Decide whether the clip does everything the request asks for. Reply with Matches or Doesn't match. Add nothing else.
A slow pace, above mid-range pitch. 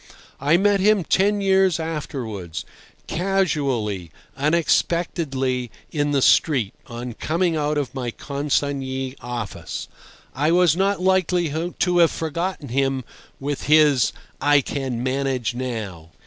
Doesn't match